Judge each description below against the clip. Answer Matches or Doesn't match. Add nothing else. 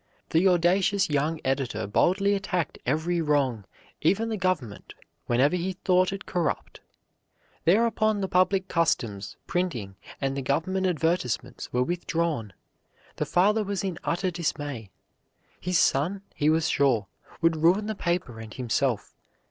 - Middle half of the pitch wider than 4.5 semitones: Matches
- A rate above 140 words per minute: Doesn't match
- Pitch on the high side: Doesn't match